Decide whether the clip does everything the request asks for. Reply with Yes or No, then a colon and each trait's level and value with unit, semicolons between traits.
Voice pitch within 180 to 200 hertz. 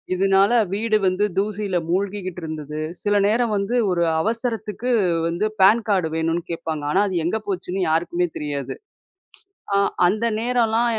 Yes: high, 195 Hz